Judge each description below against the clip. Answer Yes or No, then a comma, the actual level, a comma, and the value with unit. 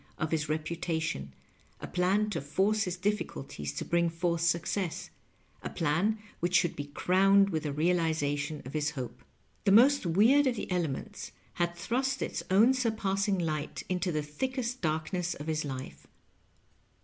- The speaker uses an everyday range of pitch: Yes, average, 4.5 semitones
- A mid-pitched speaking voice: Yes, medium, 170 Hz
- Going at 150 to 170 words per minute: Yes, average, 165 wpm